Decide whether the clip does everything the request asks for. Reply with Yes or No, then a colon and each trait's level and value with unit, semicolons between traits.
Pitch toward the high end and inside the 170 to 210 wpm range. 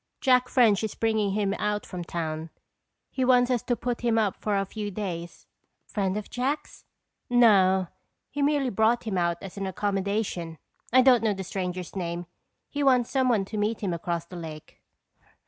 Yes: high, 205 Hz; average, 180 wpm